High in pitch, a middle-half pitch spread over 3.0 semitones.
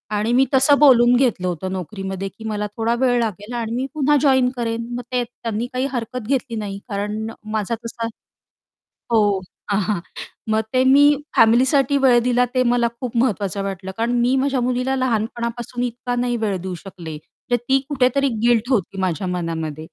Yes: high, 235 Hz; average, 3.6 semitones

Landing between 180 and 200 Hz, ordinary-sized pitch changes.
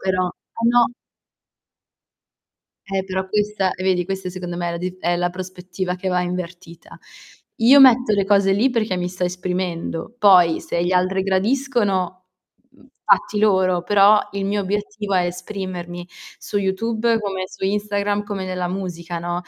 No: high, 190 Hz; narrow, 2.3 semitones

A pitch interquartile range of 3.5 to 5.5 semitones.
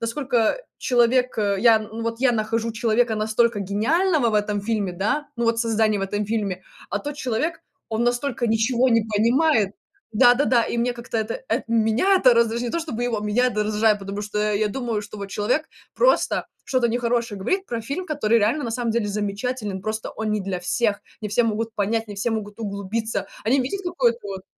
No: narrow, 2.6 semitones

